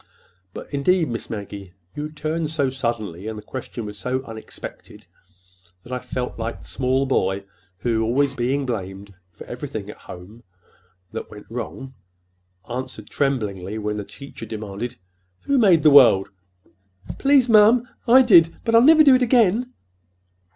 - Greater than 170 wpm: No, average, 155 wpm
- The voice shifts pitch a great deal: Yes, wide, 7.7 semitones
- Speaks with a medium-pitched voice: No, low, 130 Hz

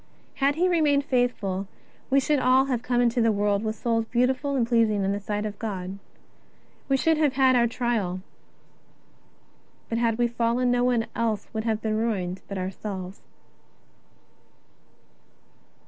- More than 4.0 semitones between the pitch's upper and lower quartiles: No, average, 3.6 semitones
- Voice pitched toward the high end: Yes, high, 230 Hz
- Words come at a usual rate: Yes, average, 150 wpm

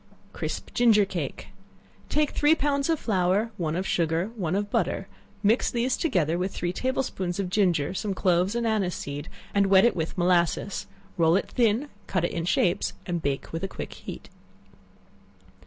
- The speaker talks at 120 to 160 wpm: No, average, 180 wpm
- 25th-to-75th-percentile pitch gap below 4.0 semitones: No, average, 4.6 semitones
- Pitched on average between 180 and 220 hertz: Yes, high, 190 Hz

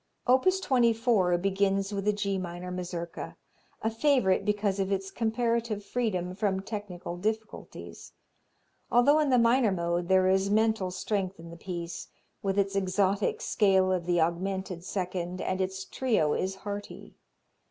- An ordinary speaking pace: Yes, average, 145 wpm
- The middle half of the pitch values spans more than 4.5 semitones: No, average, 3.1 semitones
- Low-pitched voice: No, high, 195 Hz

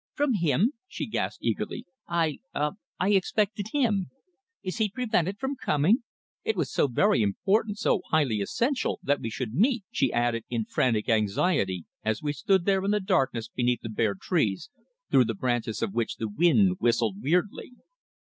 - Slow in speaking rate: No, average, 170 wpm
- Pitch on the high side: No, medium, 155 Hz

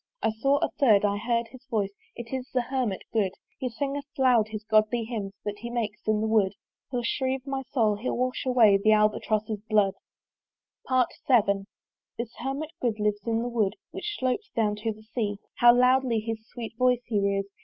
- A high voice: Yes, high, 230 Hz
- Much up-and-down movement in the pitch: No, average, 3.1 semitones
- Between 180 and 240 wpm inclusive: Yes, average, 190 wpm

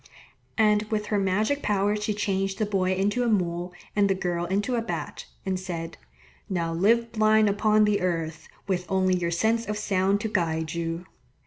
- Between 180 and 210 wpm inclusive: Yes, average, 185 wpm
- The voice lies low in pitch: No, high, 195 Hz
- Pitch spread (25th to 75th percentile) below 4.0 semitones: Yes, average, 3.0 semitones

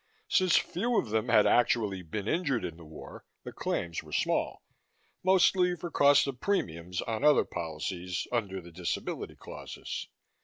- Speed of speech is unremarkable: Yes, average, 155 wpm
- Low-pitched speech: Yes, low, 110 Hz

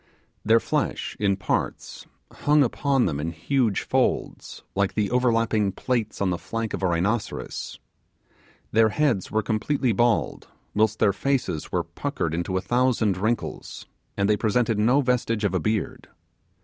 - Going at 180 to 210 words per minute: No, average, 150 wpm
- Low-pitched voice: Yes, low, 110 Hz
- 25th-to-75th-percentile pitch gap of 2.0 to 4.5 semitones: Yes, average, 3.7 semitones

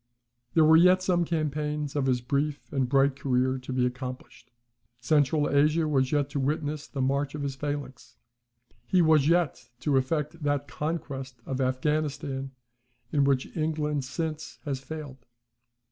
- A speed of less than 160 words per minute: Yes, average, 150 wpm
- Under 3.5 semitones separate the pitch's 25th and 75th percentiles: Yes, narrow, 2.5 semitones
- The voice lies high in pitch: No, medium, 145 Hz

